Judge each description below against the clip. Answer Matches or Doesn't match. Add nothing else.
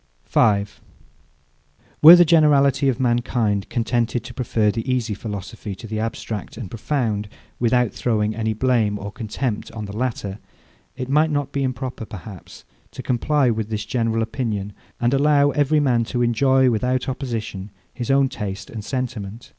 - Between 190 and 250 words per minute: Doesn't match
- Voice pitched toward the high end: Doesn't match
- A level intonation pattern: Doesn't match